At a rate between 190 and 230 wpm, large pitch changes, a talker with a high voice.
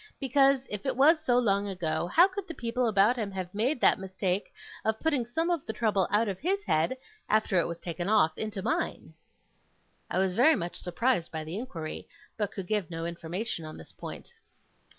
Yes: average, 200 wpm; wide, 6.1 semitones; high, 210 Hz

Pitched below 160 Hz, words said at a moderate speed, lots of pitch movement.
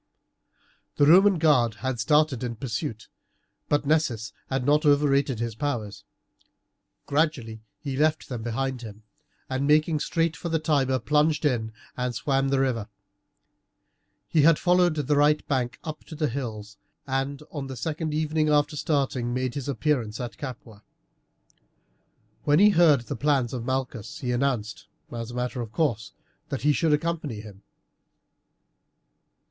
No: low, 135 Hz; average, 150 wpm; average, 4.0 semitones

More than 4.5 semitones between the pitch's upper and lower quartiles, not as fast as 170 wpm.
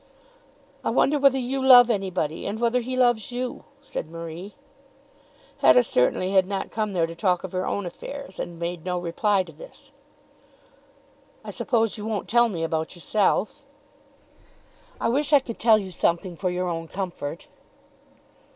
Yes: wide, 5.6 semitones; average, 160 wpm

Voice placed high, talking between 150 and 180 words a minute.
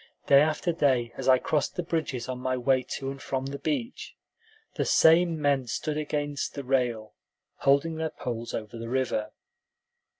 No: low, 135 Hz; average, 170 wpm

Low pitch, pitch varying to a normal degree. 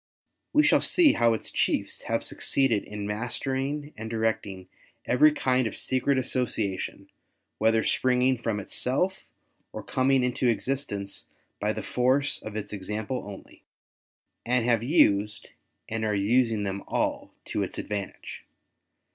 Yes: low, 115 Hz; average, 3.9 semitones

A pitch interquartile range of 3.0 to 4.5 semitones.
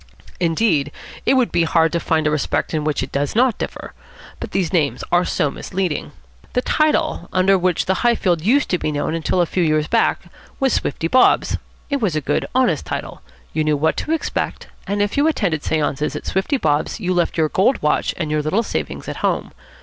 No: average, 5.1 semitones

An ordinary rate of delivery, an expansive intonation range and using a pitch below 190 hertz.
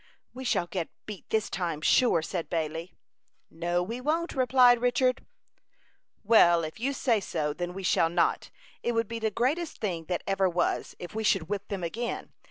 No: average, 180 wpm; wide, 5.9 semitones; high, 195 Hz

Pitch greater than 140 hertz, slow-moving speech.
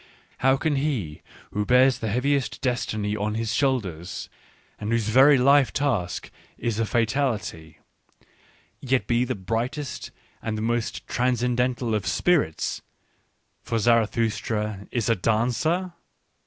No: low, 115 Hz; slow, 130 wpm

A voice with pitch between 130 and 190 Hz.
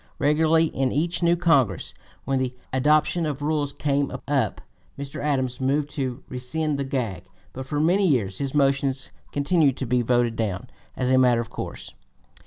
Yes: medium, 140 Hz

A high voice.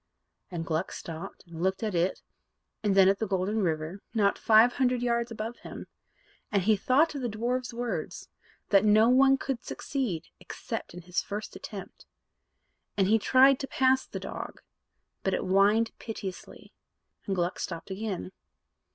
Yes: high, 210 Hz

